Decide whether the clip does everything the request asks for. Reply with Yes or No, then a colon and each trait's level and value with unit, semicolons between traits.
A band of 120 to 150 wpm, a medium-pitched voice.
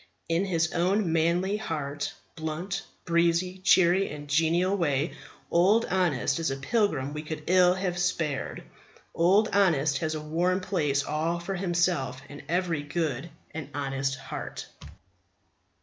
Yes: slow, 135 wpm; medium, 170 Hz